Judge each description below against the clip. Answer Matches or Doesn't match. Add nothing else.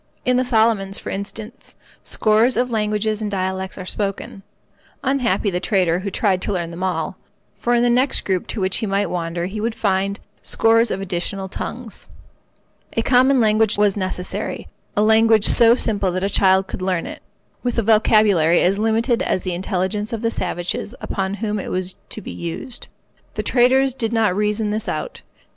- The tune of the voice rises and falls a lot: Doesn't match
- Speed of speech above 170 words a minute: Matches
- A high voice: Matches